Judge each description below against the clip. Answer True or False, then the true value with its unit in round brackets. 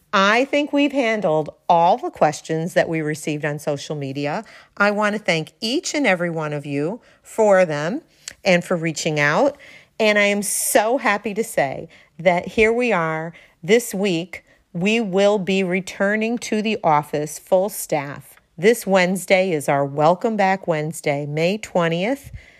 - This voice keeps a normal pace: True (160 wpm)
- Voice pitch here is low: False (185 Hz)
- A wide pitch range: True (5.7 semitones)